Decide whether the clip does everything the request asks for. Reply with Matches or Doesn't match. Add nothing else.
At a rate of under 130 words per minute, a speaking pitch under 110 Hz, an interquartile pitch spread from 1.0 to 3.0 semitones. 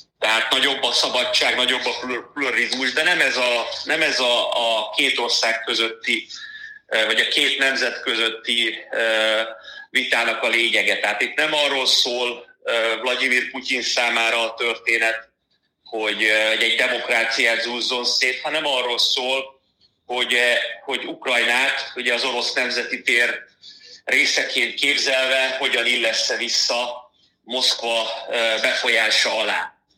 Doesn't match